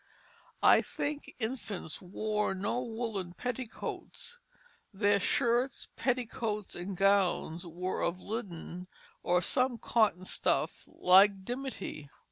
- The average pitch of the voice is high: Yes, high, 205 Hz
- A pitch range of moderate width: Yes, average, 4.7 semitones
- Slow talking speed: Yes, slow, 100 wpm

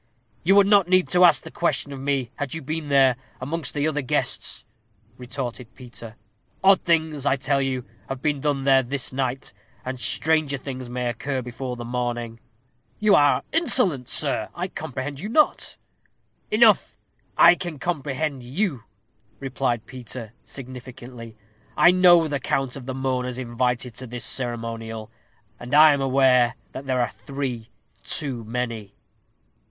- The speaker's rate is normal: Yes, average, 155 wpm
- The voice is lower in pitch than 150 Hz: Yes, low, 135 Hz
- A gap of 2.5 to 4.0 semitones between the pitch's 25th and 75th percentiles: Yes, average, 3.3 semitones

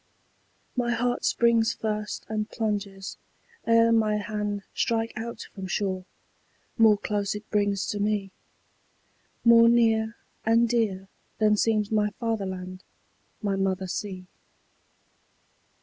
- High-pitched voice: Yes, high, 210 Hz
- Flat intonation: Yes, narrow, 2.3 semitones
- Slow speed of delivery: Yes, slow, 115 wpm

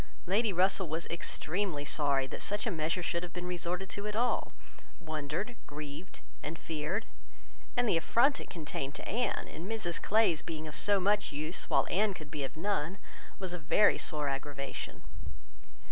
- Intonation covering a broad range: No, average, 4.8 semitones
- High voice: No, medium, 175 Hz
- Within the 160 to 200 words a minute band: Yes, average, 175 wpm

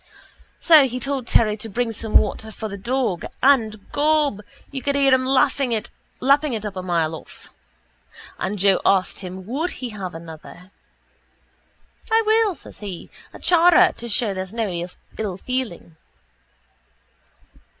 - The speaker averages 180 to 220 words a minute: No, average, 145 wpm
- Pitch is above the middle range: Yes, high, 225 Hz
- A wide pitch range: Yes, wide, 6.1 semitones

